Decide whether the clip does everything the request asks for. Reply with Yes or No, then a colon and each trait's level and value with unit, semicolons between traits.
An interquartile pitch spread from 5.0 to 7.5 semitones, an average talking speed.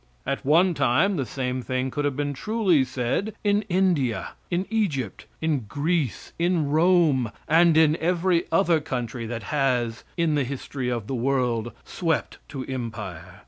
Yes: wide, 5.4 semitones; average, 150 wpm